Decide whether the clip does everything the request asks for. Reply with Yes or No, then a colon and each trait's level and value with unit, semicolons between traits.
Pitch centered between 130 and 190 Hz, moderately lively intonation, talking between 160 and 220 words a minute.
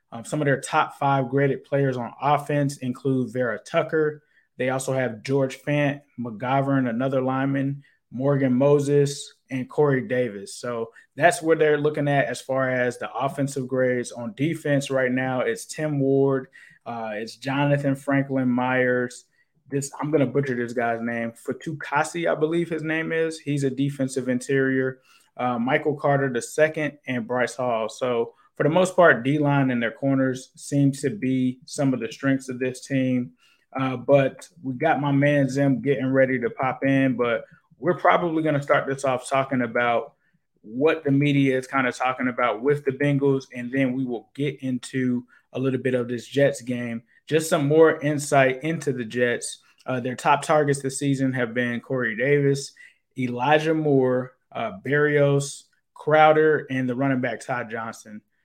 No: low, 135 Hz; narrow, 2.3 semitones; average, 170 wpm